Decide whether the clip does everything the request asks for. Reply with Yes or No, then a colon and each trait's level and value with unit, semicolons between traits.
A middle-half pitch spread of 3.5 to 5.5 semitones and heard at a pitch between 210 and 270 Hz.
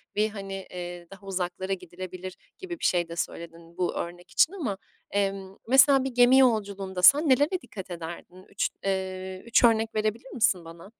No: average, 4.5 semitones; high, 195 Hz